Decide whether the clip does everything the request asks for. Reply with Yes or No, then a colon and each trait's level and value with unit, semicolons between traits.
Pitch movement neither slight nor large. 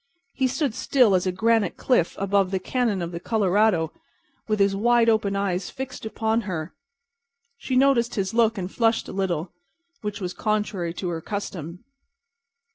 Yes: average, 3.8 semitones